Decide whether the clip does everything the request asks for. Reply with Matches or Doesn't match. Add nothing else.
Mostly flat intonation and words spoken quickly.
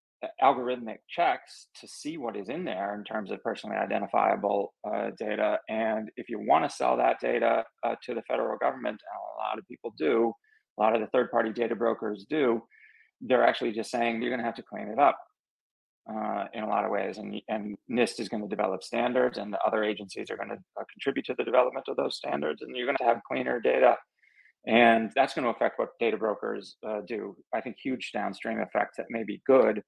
Matches